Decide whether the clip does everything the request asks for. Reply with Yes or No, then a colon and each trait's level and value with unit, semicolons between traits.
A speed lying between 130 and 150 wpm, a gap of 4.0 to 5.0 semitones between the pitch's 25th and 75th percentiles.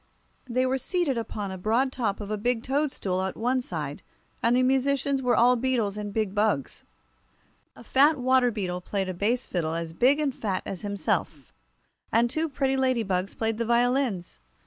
No: average, 180 wpm; average, 4.7 semitones